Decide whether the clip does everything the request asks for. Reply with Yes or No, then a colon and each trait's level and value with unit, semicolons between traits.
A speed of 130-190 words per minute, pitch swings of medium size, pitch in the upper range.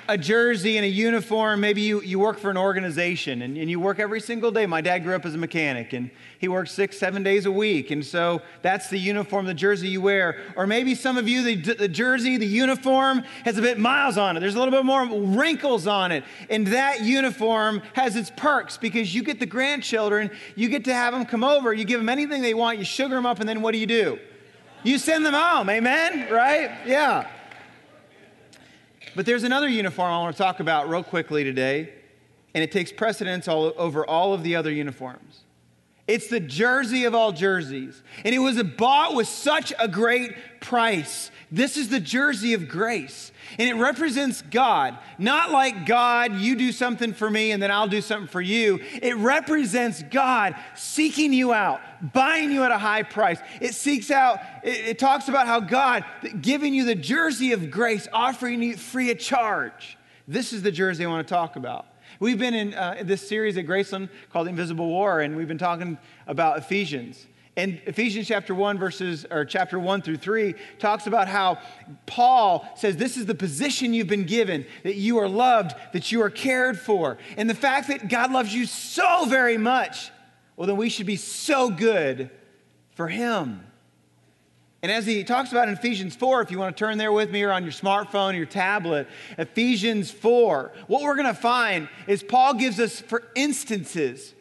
No: average, 200 wpm; average, 4.9 semitones; high, 220 Hz